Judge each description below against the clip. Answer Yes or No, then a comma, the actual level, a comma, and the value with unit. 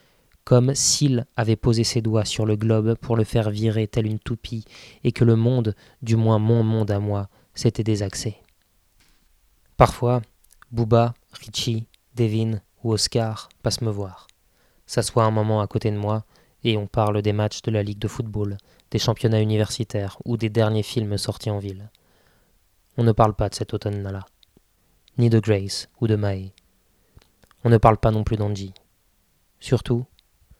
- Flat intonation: Yes, narrow, 2.2 semitones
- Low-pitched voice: Yes, low, 110 Hz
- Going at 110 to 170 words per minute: Yes, average, 165 wpm